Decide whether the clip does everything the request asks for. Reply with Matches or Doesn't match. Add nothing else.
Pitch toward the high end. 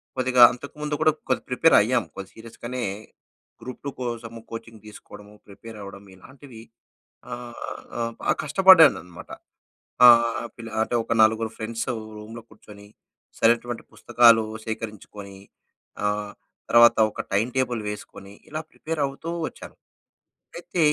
Doesn't match